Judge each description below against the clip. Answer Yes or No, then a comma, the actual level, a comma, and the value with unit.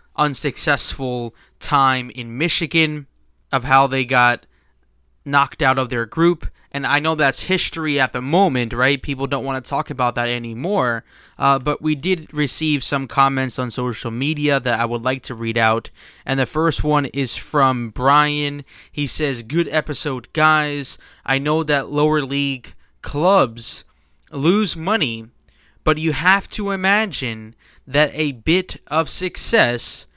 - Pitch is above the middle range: No, medium, 140 Hz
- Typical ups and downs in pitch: Yes, average, 3.8 semitones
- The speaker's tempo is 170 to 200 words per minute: No, average, 155 wpm